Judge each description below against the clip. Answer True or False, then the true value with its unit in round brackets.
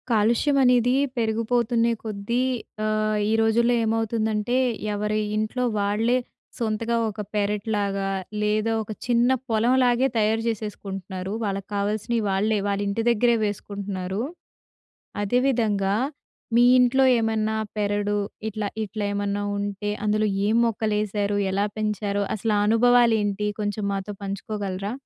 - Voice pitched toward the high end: True (215 Hz)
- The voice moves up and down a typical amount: False (2.0 semitones)